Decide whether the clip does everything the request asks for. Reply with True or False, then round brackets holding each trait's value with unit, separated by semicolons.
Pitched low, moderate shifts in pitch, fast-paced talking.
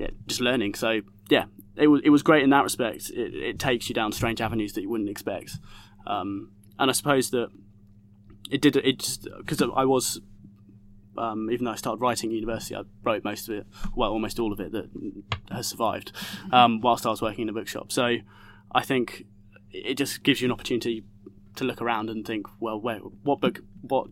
True (110 Hz; 3.6 semitones; 210 wpm)